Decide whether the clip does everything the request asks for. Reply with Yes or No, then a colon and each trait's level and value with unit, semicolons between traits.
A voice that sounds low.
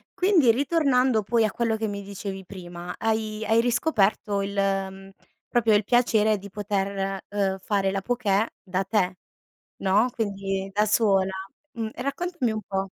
No: high, 205 Hz